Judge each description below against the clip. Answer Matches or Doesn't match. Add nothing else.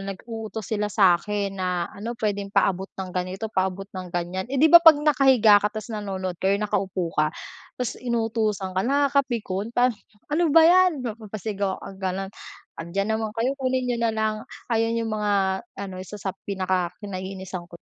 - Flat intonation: Doesn't match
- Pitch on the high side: Matches